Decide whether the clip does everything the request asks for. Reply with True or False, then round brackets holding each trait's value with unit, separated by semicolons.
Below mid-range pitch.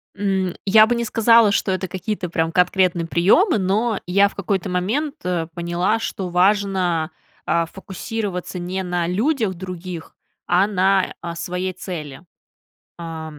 False (185 Hz)